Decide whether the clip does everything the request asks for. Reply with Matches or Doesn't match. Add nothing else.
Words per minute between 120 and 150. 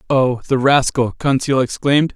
Matches